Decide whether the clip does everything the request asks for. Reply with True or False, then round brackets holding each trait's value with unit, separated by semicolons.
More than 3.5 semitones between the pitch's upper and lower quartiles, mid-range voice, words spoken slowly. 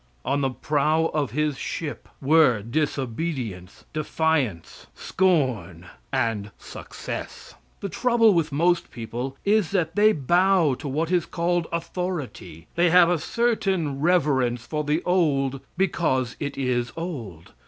True (5.1 semitones; 150 Hz; 130 wpm)